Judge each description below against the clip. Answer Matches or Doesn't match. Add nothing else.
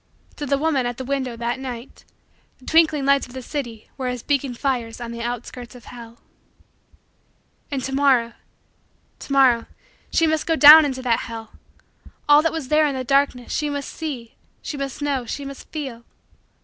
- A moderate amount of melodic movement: Matches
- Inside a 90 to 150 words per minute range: Doesn't match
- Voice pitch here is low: Doesn't match